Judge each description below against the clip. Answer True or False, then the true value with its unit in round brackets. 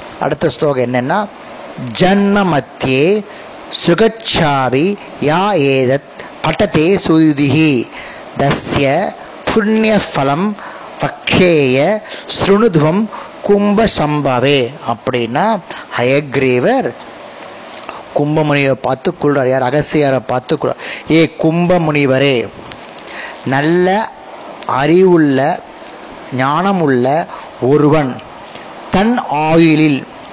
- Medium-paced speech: False (60 wpm)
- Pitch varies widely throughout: True (6.0 semitones)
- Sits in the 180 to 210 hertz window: False (155 Hz)